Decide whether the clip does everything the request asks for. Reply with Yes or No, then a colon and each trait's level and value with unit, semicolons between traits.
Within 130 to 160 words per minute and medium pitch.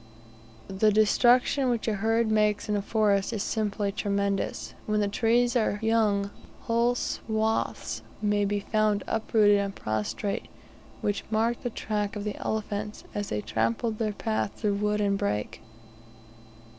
No: average, 145 wpm; high, 210 Hz